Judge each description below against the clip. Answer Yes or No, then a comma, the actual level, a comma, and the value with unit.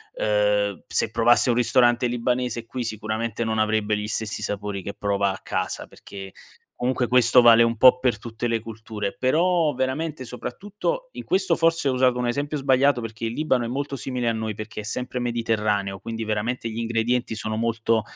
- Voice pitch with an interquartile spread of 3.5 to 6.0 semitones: No, average, 2.7 semitones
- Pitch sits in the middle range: No, low, 115 Hz